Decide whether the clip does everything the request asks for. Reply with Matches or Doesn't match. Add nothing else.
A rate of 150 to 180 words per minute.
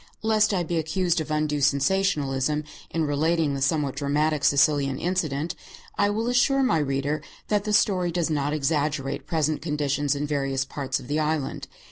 Matches